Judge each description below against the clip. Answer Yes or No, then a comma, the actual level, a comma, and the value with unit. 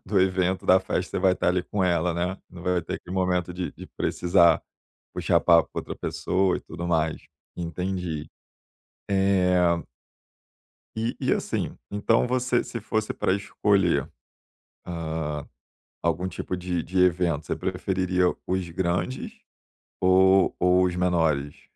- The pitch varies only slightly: Yes, narrow, 1.6 semitones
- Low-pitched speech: Yes, very low, 90 Hz